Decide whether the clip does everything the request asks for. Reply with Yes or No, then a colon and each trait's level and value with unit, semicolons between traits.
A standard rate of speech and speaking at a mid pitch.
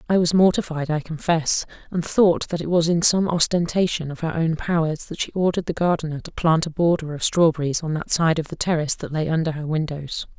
No: fast, 225 wpm; medium, 165 Hz